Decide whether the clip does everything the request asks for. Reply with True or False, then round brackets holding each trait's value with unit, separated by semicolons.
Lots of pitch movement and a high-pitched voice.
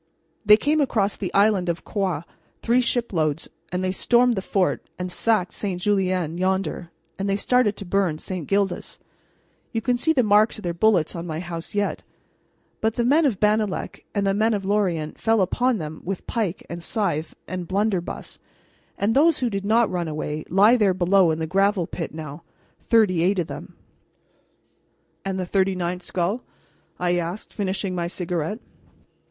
False (3.5 semitones; 195 Hz)